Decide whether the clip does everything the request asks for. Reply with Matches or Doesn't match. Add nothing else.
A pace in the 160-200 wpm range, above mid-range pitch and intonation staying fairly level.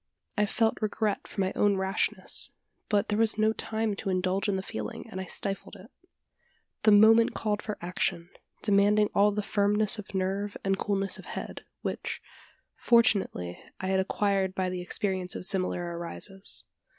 Matches